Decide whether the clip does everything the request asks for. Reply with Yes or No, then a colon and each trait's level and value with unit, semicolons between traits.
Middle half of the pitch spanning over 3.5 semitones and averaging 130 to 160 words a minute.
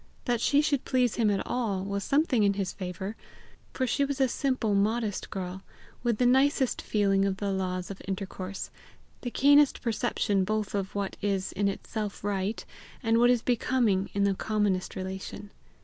No: average, 4.0 semitones; average, 175 wpm